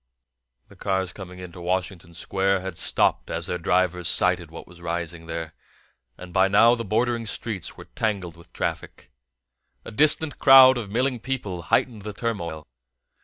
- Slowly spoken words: No, average, 160 wpm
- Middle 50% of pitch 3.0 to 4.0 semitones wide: No, average, 4.7 semitones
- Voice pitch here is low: Yes, very low, 95 Hz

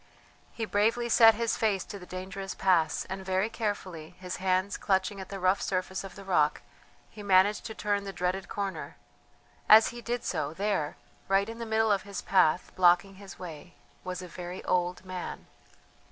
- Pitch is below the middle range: No, high, 190 Hz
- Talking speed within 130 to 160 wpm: No, average, 180 wpm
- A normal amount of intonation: No, narrow, 2.1 semitones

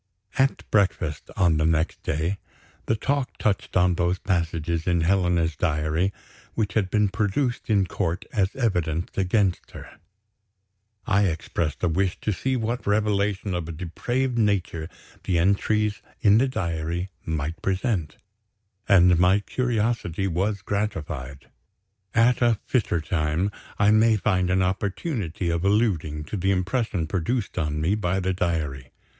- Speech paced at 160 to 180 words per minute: No, average, 140 wpm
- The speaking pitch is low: Yes, very low, 95 Hz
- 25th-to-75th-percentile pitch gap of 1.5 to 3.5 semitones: No, average, 4.1 semitones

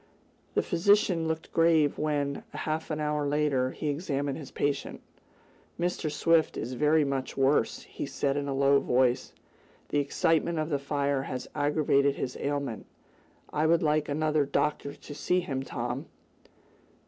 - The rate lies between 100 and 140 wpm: No, average, 150 wpm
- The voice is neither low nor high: Yes, medium, 145 Hz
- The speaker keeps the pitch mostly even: Yes, narrow, 2.0 semitones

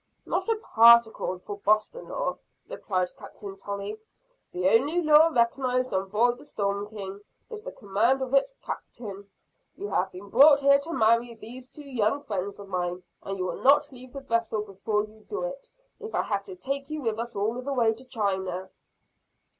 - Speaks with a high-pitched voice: Yes, high, 230 Hz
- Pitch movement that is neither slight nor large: No, wide, 5.7 semitones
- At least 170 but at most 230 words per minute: Yes, average, 185 wpm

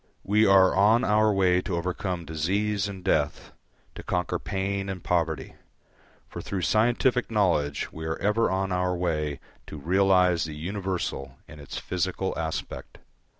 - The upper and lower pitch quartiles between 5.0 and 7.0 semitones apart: No, average, 3.4 semitones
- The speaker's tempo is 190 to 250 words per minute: No, average, 150 wpm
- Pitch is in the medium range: No, very low, 90 Hz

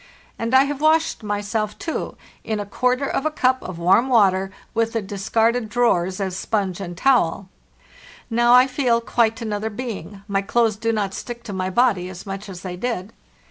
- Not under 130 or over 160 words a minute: No, average, 185 wpm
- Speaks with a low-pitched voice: No, high, 220 Hz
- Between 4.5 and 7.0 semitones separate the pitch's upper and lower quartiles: No, average, 3.9 semitones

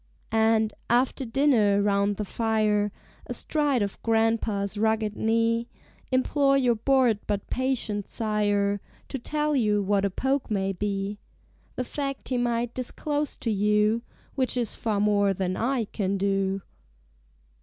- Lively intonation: No, average, 3.5 semitones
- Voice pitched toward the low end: No, high, 220 Hz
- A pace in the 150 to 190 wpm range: No, slow, 135 wpm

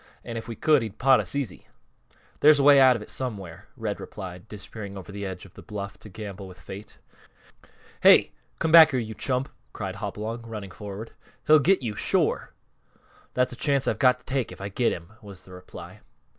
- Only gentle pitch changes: No, average, 4.8 semitones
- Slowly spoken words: No, fast, 205 wpm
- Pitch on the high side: No, low, 110 Hz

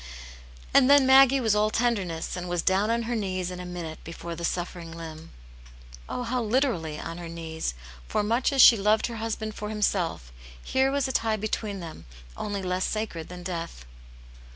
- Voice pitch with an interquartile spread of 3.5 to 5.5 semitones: Yes, average, 5.2 semitones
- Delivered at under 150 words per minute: No, average, 185 wpm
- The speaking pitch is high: Yes, high, 200 Hz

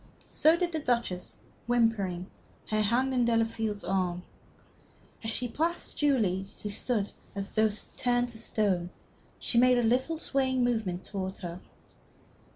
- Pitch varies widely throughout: No, average, 4.3 semitones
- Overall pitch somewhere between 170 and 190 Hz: No, high, 225 Hz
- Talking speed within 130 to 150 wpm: Yes, average, 140 wpm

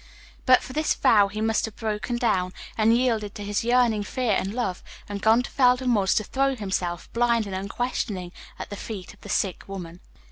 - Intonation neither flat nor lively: Yes, average, 3.5 semitones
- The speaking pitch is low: No, high, 215 Hz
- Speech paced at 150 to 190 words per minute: No, fast, 205 wpm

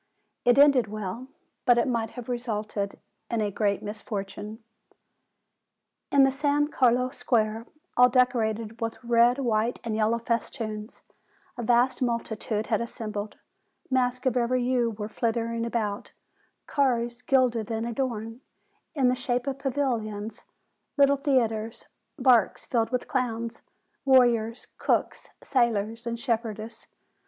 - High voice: Yes, high, 235 Hz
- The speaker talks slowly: Yes, slow, 130 wpm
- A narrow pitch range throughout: Yes, narrow, 2.3 semitones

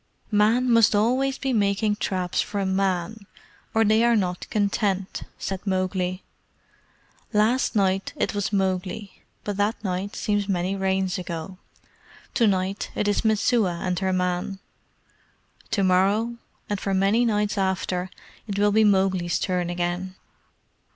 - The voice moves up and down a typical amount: No, narrow, 2.1 semitones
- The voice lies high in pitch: Yes, high, 195 Hz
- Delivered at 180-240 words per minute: No, average, 140 wpm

